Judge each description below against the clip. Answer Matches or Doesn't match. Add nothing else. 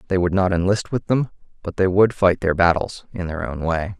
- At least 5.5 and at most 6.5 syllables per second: Doesn't match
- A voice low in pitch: Matches